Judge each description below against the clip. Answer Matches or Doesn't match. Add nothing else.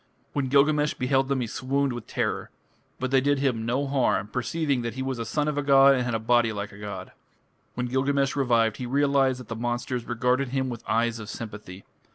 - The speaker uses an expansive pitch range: Doesn't match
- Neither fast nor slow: Doesn't match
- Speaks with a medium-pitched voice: Doesn't match